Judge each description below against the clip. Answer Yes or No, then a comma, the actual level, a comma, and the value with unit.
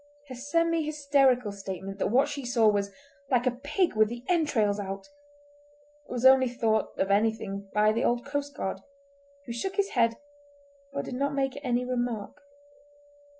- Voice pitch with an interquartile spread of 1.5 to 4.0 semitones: No, average, 4.8 semitones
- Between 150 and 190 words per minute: Yes, average, 155 wpm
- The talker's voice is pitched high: Yes, high, 245 Hz